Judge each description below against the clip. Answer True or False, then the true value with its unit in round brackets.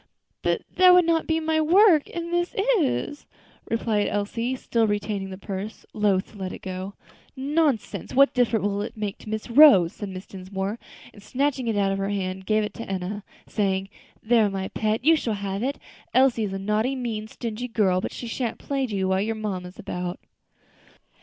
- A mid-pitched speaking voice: False (215 Hz)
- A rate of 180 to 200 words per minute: True (195 wpm)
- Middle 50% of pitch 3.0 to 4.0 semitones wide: False (4.8 semitones)